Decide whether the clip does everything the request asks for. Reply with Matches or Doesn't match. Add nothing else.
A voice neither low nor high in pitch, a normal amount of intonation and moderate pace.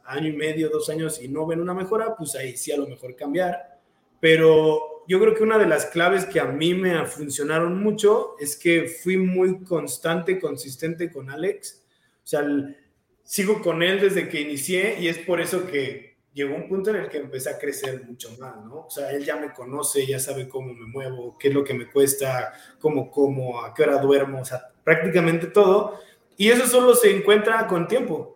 Doesn't match